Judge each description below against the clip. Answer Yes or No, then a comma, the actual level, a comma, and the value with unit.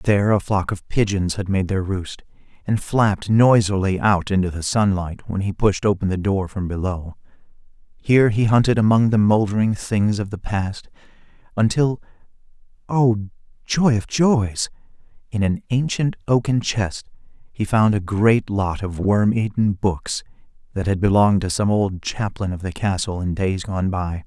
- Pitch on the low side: Yes, low, 100 Hz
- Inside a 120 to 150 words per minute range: No, average, 165 wpm